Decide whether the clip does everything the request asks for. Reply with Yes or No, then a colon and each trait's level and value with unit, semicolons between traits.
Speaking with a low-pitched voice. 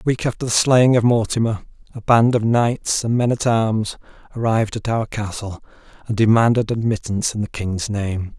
Yes: low, 110 Hz